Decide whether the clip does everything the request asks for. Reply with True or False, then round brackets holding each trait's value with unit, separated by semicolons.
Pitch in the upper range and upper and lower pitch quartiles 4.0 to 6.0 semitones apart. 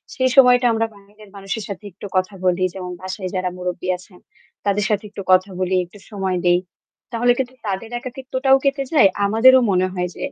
True (200 Hz; 4.8 semitones)